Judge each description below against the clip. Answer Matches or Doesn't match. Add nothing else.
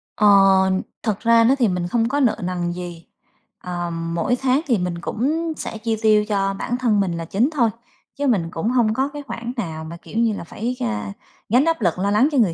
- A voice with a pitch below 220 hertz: Matches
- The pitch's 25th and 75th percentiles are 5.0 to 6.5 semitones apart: Matches